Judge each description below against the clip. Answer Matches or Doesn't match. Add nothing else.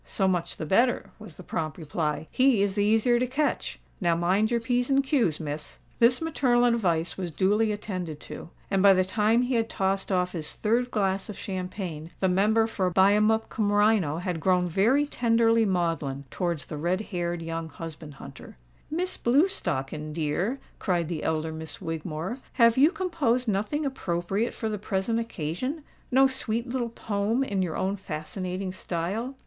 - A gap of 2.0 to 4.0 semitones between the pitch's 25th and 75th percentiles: Doesn't match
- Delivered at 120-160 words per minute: Doesn't match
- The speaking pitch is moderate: Doesn't match